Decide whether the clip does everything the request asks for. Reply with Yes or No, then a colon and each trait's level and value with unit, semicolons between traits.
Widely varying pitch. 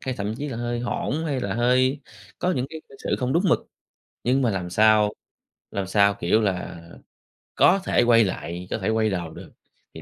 No: average, 4.5 semitones